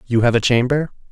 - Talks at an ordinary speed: No, fast, 215 wpm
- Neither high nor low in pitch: No, low, 125 Hz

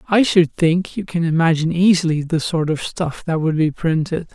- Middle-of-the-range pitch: Yes, medium, 170 Hz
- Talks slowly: No, fast, 205 wpm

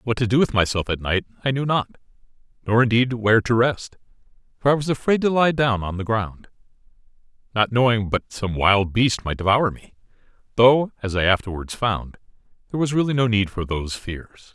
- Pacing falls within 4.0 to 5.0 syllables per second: No, 5.4 syllables/s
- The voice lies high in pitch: No, low, 115 Hz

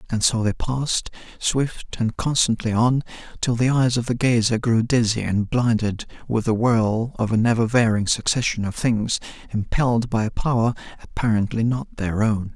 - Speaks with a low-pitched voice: Yes, low, 115 Hz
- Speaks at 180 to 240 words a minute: No, average, 170 wpm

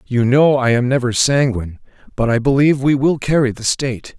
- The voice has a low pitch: Yes, low, 130 Hz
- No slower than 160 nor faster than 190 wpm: No, average, 200 wpm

